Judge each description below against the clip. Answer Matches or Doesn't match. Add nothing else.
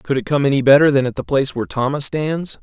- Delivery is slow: Doesn't match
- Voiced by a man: Matches